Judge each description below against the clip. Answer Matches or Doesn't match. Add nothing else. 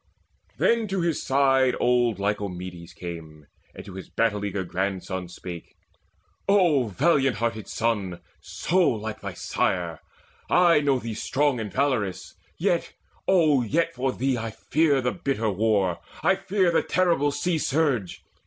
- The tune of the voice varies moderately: Doesn't match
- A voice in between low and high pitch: Doesn't match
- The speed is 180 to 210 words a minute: Doesn't match